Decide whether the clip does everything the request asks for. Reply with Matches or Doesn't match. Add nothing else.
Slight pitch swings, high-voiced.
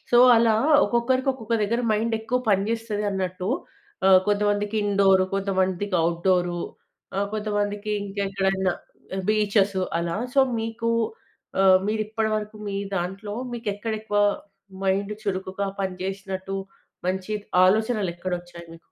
Matches